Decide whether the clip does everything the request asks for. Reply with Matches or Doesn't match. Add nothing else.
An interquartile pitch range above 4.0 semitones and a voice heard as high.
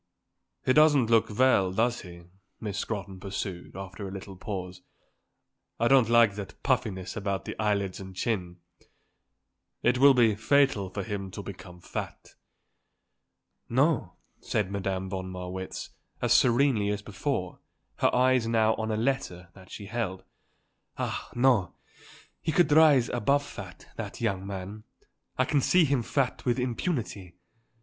Doesn't match